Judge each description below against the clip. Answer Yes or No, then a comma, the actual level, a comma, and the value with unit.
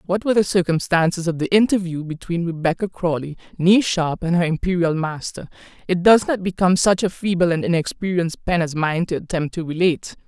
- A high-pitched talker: No, medium, 175 Hz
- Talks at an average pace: Yes, average, 185 wpm